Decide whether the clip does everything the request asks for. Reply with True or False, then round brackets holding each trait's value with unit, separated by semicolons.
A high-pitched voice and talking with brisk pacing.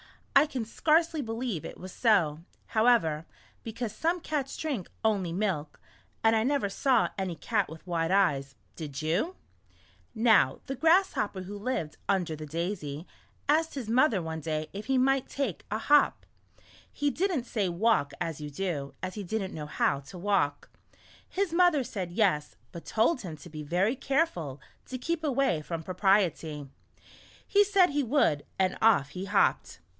False (200 Hz; 165 wpm)